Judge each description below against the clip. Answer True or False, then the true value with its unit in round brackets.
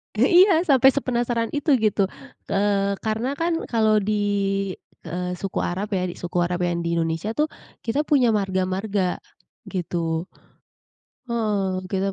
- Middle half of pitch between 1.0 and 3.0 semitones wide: False (4.2 semitones)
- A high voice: True (205 Hz)